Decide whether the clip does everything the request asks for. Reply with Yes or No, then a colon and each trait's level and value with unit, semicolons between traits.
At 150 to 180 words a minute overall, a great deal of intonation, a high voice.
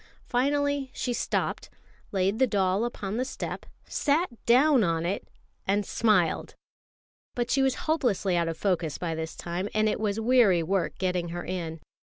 Yes: average, 165 wpm; wide, 5.9 semitones; high, 205 Hz